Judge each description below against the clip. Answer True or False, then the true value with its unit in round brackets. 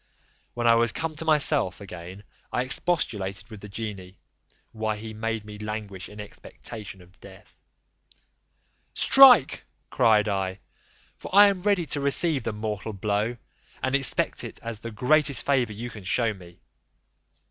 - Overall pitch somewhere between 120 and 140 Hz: False (110 Hz)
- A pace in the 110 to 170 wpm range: True (150 wpm)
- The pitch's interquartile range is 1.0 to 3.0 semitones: False (4.4 semitones)